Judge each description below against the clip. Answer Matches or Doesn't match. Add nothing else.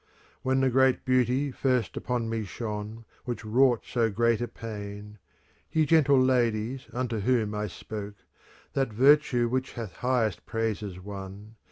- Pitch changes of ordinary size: Matches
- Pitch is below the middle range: Matches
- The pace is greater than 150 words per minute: Matches